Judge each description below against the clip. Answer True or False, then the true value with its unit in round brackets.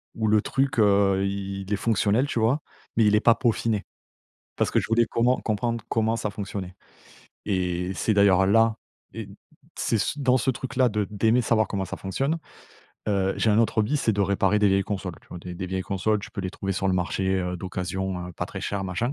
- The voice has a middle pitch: False (100 Hz)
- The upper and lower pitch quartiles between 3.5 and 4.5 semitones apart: False (2.9 semitones)